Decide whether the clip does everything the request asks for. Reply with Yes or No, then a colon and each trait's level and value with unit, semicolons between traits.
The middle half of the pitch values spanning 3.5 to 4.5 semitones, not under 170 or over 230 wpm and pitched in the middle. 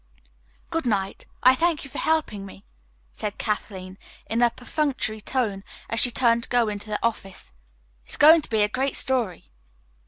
No: average, 4.0 semitones; average, 180 wpm; high, 230 Hz